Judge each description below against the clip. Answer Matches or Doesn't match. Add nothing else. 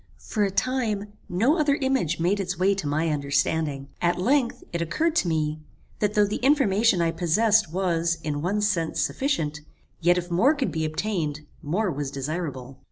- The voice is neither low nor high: Matches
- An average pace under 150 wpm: Doesn't match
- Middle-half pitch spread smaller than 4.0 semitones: Doesn't match